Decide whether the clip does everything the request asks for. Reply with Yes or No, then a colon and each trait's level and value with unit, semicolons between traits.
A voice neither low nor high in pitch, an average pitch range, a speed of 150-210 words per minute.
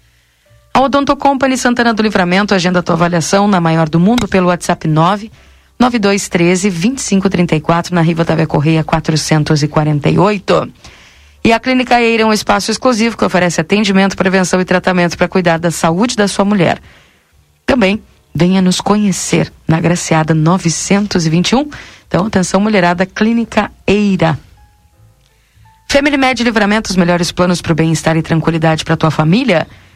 No: medium, 180 Hz; average, 4.1 semitones; average, 140 wpm